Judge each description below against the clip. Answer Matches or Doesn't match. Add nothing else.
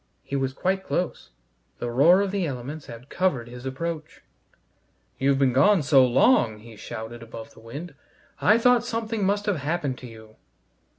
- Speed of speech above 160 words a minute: Matches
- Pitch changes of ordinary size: Doesn't match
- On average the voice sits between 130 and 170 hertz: Matches